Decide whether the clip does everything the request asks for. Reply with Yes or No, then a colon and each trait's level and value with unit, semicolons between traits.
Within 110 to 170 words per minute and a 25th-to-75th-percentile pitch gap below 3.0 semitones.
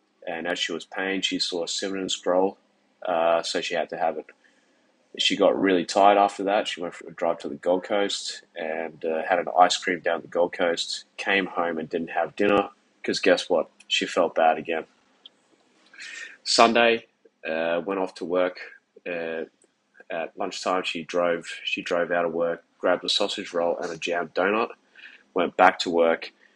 No: average, 190 wpm; narrow, 2.5 semitones